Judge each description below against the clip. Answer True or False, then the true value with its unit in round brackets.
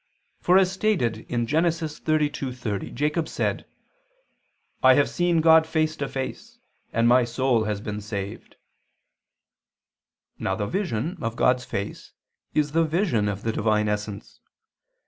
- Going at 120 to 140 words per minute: True (135 wpm)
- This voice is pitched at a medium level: False (130 Hz)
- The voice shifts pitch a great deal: True (6.6 semitones)